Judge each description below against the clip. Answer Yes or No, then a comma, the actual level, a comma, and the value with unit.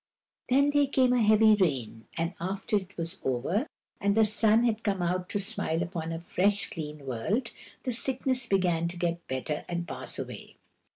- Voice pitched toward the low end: No, high, 190 Hz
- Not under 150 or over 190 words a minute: Yes, average, 180 wpm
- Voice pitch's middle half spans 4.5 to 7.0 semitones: Yes, average, 4.9 semitones